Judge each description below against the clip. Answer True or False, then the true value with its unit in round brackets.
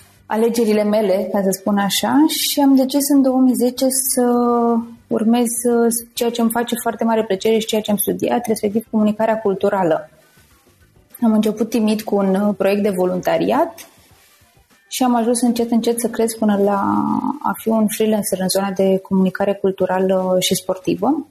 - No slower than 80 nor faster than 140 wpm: False (160 wpm)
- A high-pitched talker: True (220 Hz)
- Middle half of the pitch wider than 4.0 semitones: False (3.0 semitones)